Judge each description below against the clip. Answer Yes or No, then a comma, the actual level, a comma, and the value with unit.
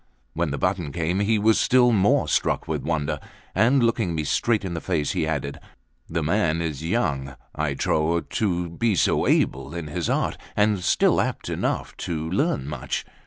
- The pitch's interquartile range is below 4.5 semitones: No, average, 5.2 semitones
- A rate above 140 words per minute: Yes, average, 180 wpm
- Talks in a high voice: No, very low, 85 Hz